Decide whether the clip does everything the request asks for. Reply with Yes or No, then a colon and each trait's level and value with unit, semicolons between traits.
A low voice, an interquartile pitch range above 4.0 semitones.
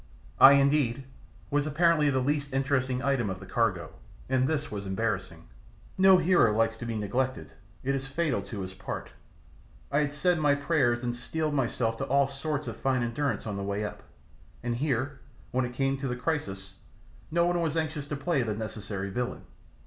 Yes: low, 130 Hz; average, 4.5 semitones